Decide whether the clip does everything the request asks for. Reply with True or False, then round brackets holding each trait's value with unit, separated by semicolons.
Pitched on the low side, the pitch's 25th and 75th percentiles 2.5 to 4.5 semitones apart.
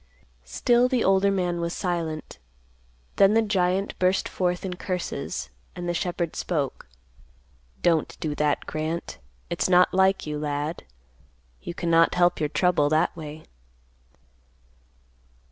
False (175 Hz; 3.1 semitones)